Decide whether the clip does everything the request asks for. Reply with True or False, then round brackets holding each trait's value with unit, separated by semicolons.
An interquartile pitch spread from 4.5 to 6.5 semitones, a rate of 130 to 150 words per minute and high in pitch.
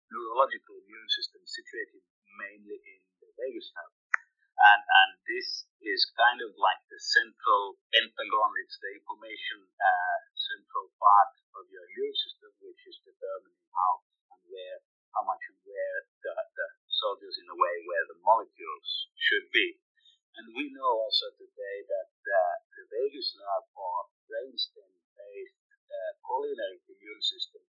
False (3.5 semitones; 145 wpm; 395 Hz)